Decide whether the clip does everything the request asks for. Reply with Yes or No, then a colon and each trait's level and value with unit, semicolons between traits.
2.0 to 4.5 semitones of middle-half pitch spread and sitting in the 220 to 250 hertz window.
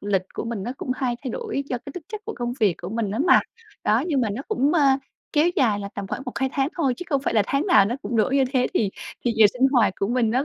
Yes: average, 4.2 semitones; high, 245 Hz